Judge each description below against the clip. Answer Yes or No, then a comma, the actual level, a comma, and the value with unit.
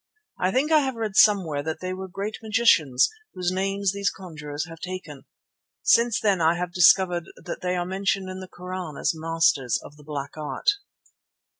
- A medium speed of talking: Yes, average, 180 wpm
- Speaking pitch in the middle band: Yes, medium, 180 Hz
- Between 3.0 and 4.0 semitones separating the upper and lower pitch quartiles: Yes, average, 3.5 semitones